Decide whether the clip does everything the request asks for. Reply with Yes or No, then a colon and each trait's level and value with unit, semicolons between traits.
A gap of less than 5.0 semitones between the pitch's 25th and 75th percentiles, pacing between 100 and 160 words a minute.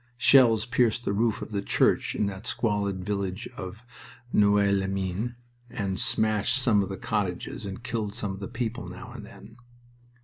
No: average, 2.8 semitones; average, 175 wpm